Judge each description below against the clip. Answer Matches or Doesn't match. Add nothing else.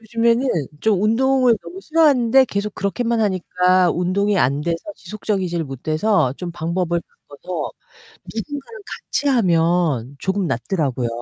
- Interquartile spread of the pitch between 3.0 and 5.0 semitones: Doesn't match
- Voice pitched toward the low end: Doesn't match